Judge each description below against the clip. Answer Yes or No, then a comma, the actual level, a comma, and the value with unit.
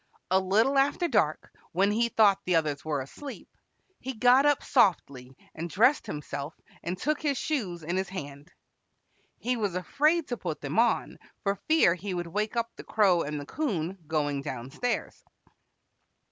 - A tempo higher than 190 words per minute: No, average, 170 wpm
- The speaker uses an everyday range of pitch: No, wide, 7.5 semitones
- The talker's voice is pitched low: No, high, 190 Hz